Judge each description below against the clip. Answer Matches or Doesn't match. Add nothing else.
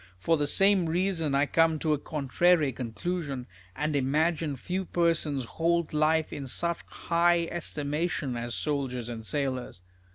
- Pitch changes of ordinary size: Matches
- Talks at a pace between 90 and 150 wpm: Matches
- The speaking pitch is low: Doesn't match